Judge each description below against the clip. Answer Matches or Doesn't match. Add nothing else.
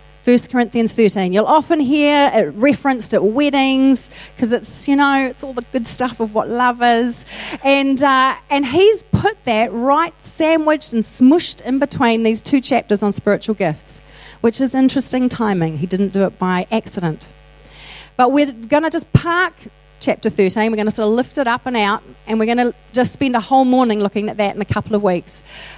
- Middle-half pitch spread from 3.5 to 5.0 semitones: Matches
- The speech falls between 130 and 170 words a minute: Doesn't match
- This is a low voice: Doesn't match